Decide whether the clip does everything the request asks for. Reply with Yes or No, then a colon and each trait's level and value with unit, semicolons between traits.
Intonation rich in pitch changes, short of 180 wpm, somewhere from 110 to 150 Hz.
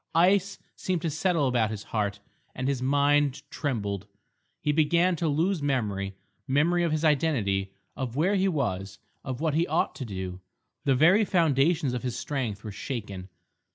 Yes: wide, 6.9 semitones; average, 160 wpm; medium, 140 Hz